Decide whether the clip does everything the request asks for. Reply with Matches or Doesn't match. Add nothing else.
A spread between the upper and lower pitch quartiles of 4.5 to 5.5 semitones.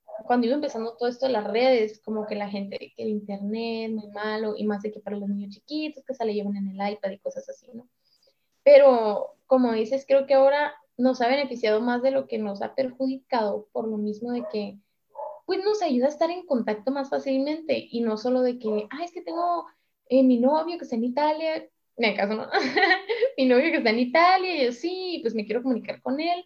Matches